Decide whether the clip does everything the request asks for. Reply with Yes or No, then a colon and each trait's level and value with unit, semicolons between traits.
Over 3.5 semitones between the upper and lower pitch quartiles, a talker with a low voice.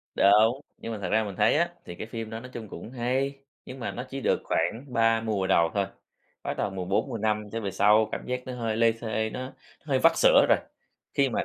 No: average, 3.1 semitones; low, 115 Hz